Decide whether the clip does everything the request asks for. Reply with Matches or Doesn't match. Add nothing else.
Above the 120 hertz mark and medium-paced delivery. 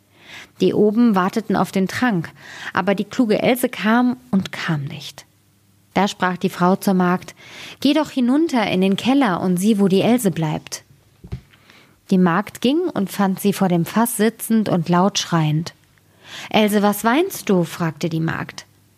Matches